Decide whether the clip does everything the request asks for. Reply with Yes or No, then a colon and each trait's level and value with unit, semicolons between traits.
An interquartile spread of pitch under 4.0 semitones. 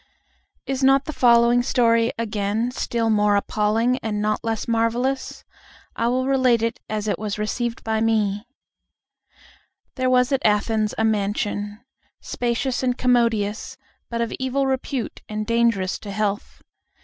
Yes: average, 2.8 semitones